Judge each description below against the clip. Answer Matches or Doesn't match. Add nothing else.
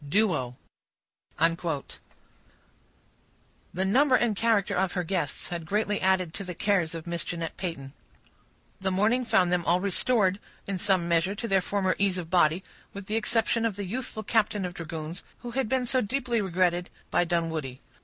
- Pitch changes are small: Doesn't match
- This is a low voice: Doesn't match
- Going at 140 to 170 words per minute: Matches